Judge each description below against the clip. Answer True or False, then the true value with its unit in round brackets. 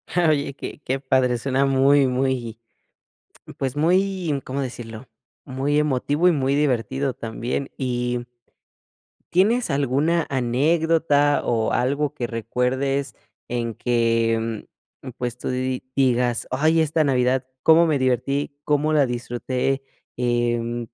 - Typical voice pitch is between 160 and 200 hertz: False (130 Hz)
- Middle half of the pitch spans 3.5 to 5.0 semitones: False (3.0 semitones)